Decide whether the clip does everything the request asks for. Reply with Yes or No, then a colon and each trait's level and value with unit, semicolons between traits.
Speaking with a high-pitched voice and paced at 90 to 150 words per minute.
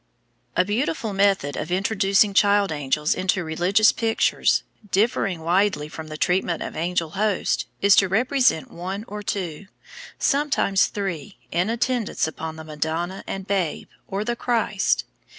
Yes: high, 195 Hz; average, 140 wpm